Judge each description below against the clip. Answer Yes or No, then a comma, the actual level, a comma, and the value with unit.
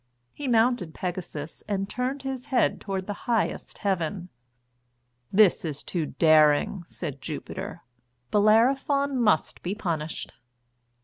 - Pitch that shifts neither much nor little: No, wide, 6.4 semitones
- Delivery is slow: Yes, slow, 120 wpm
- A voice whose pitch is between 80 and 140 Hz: No, high, 195 Hz